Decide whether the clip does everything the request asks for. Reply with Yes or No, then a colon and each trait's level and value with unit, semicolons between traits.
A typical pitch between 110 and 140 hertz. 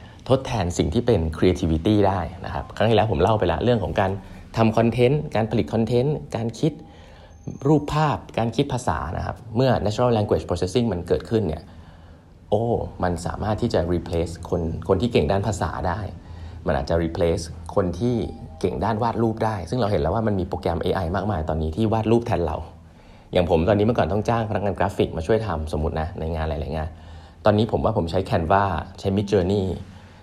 No: low, 100 Hz